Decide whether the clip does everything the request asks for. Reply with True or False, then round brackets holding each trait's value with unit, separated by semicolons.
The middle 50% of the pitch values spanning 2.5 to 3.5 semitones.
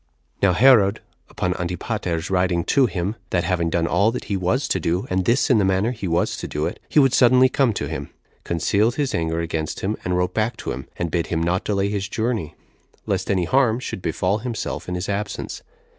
False (4.5 semitones)